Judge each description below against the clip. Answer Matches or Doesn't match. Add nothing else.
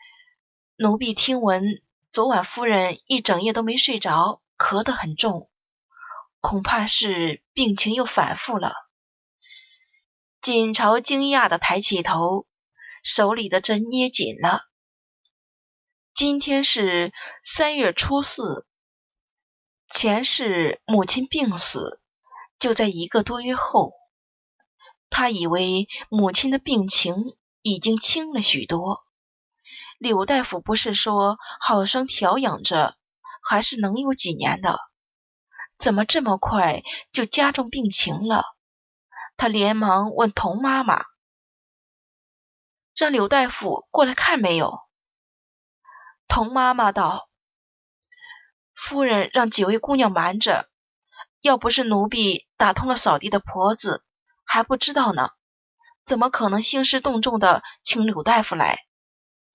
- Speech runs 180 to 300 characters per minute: Doesn't match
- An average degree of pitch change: Matches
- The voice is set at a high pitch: Matches